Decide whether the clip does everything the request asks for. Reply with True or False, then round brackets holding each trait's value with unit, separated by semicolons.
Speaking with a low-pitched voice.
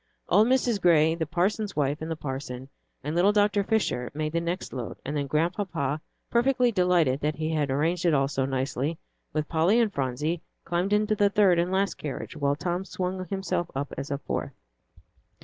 False (165 Hz)